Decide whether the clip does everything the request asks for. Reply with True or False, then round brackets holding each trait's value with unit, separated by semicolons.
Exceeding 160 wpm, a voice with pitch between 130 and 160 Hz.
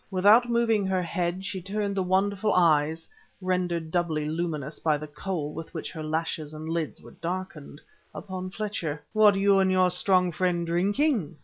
False (170 wpm; 180 Hz)